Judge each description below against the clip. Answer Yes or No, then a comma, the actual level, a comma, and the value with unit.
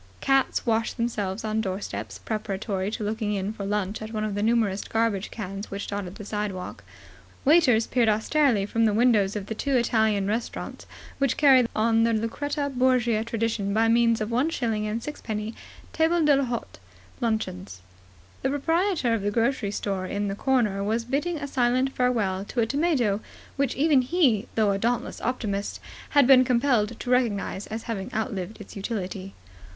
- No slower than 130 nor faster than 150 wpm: No, average, 170 wpm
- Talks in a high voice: Yes, high, 225 Hz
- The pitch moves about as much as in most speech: Yes, average, 3.5 semitones